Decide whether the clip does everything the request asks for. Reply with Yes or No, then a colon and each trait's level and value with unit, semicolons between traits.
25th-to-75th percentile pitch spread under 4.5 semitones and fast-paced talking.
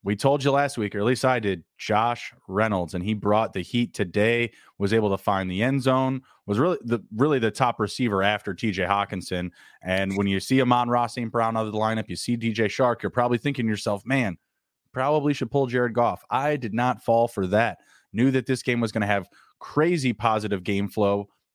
Yes: average, 3.7 semitones; fast, 225 wpm